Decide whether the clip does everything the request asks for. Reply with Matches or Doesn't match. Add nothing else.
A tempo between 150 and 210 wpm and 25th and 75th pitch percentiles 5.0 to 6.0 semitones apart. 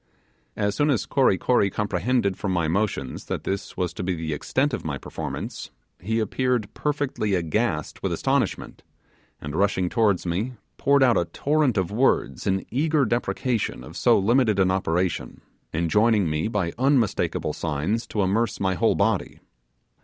Matches